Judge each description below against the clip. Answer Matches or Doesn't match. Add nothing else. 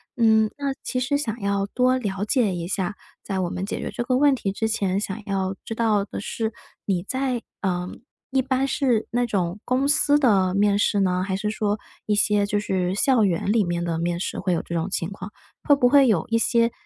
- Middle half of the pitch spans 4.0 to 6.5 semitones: Matches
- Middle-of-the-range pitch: Doesn't match